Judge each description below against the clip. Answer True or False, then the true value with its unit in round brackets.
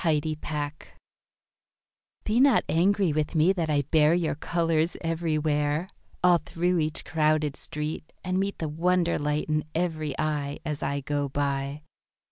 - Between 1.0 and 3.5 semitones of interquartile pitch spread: True (2.4 semitones)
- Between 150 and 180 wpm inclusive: False (140 wpm)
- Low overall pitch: False (155 Hz)